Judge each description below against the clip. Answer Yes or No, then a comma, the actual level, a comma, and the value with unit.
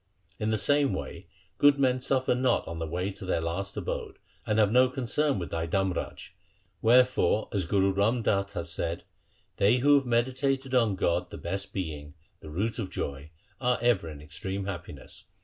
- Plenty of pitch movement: Yes, wide, 6.5 semitones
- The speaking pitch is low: Yes, low, 100 Hz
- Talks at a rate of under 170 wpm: No, average, 185 wpm